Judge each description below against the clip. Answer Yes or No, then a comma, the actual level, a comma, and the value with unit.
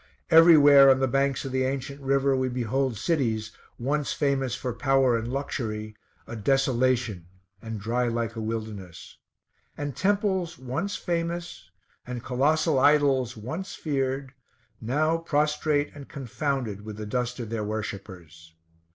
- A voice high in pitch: No, low, 130 Hz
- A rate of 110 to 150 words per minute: Yes, slow, 135 wpm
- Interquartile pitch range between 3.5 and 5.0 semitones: Yes, average, 4.2 semitones